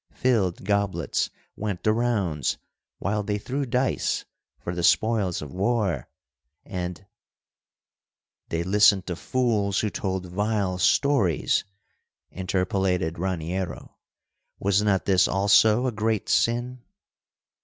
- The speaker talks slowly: Yes, slow, 110 wpm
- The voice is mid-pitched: No, low, 100 Hz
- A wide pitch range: No, average, 3.3 semitones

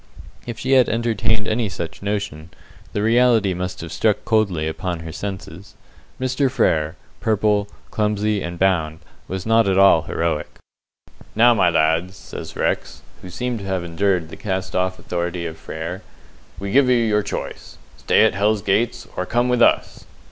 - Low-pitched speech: Yes, low, 100 Hz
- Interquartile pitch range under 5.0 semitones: Yes, average, 4.2 semitones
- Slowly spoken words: No, average, 165 wpm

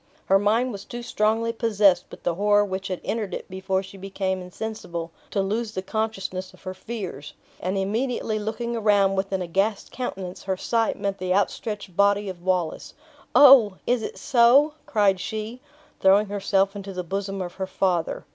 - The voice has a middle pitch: No, high, 200 Hz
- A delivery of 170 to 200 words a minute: Yes, average, 175 wpm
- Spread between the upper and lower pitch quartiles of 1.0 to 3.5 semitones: Yes, narrow, 2.6 semitones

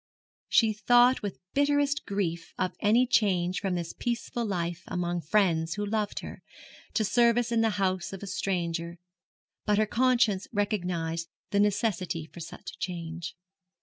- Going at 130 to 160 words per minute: Yes, average, 150 wpm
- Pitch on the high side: Yes, high, 200 Hz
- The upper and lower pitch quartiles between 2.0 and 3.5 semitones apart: No, average, 4.3 semitones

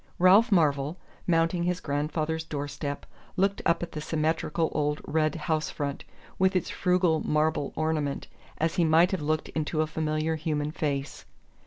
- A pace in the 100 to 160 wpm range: Yes, average, 155 wpm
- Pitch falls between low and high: Yes, medium, 155 Hz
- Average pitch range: No, narrow, 1.9 semitones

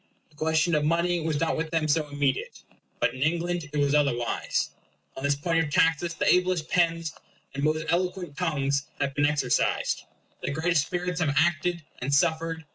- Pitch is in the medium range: Yes, medium, 160 Hz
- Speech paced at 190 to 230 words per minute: No, average, 180 wpm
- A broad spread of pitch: No, average, 2.9 semitones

